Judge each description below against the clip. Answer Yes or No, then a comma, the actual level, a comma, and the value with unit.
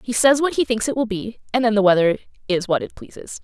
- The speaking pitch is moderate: No, high, 225 Hz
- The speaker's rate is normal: No, fast, 280 wpm